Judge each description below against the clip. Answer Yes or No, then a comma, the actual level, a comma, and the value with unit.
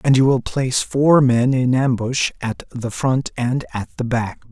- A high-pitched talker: No, low, 125 Hz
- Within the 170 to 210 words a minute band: Yes, average, 200 wpm